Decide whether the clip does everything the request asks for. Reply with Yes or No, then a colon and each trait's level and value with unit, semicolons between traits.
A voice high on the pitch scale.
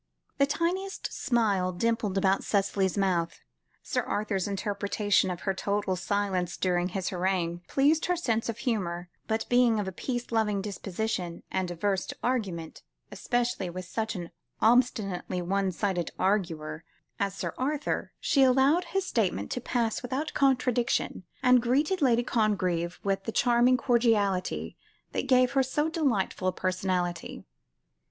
Yes: high, 205 Hz